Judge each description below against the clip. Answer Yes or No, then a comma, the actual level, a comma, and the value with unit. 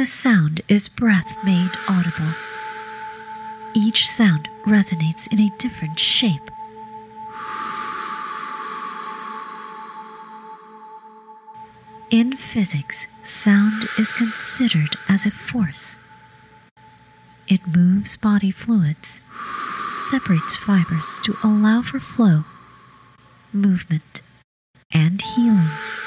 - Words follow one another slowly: Yes, slow, 80 wpm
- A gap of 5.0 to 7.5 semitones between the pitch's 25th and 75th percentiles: No, average, 3.2 semitones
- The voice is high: Yes, high, 220 Hz